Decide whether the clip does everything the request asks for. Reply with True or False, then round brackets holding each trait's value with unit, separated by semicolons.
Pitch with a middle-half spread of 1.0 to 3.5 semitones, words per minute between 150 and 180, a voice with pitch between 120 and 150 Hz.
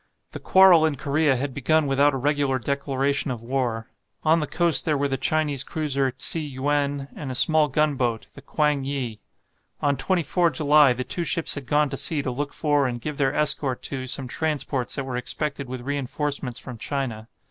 False (2.4 semitones; 190 wpm; 140 Hz)